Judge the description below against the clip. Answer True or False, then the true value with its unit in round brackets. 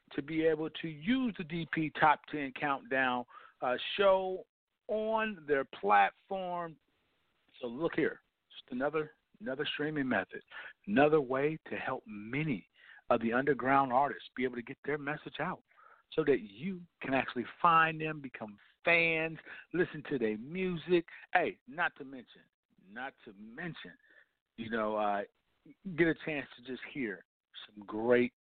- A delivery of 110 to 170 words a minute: True (150 wpm)